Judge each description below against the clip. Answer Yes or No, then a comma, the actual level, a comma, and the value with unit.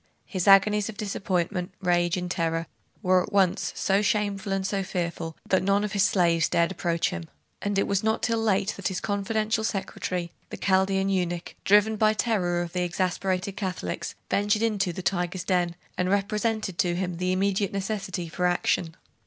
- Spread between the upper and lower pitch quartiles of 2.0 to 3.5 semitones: Yes, narrow, 2.4 semitones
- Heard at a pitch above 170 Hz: Yes, high, 190 Hz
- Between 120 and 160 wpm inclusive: No, average, 180 wpm